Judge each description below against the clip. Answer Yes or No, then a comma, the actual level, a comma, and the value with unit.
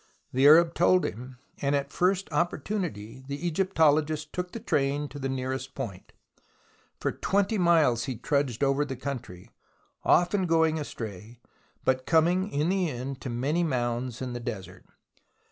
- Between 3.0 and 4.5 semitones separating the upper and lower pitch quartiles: No, average, 5.0 semitones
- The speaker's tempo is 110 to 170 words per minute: Yes, average, 155 wpm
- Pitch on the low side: No, medium, 145 Hz